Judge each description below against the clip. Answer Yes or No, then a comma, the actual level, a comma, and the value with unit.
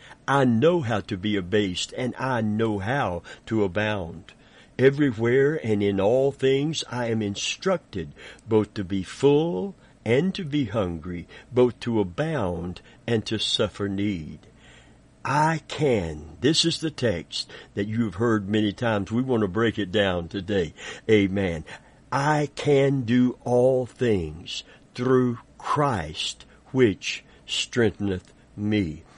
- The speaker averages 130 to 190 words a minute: Yes, slow, 135 wpm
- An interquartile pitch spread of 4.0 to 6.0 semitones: Yes, average, 4.5 semitones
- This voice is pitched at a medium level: No, low, 110 Hz